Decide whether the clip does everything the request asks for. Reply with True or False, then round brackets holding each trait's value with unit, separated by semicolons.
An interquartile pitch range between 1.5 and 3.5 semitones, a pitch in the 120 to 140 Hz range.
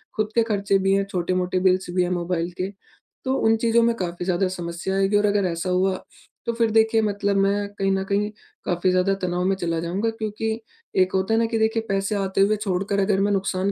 False (2.5 semitones; 195 Hz)